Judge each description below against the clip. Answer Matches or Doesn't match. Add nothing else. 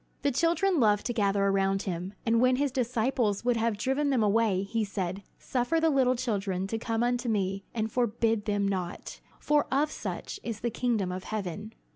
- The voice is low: Doesn't match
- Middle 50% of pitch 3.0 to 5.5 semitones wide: Matches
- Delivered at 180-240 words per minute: Matches